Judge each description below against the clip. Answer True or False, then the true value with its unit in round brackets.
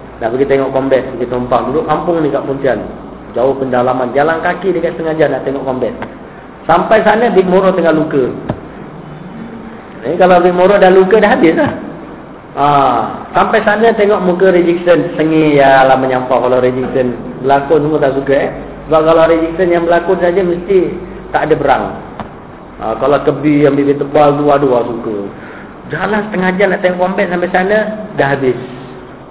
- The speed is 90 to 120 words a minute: False (165 wpm)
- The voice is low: False (160 Hz)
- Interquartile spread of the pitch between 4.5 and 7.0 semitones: True (5.3 semitones)